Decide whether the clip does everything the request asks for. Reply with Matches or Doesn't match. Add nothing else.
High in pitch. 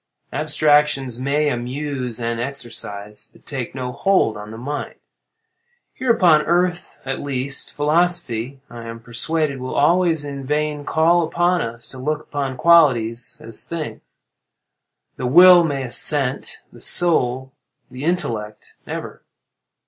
Doesn't match